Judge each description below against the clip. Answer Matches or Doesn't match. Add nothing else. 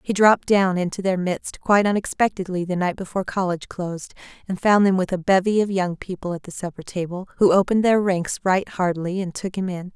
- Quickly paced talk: Matches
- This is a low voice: Doesn't match